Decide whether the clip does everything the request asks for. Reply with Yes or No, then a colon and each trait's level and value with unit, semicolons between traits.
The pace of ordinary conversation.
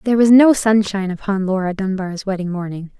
Yes: average, 180 wpm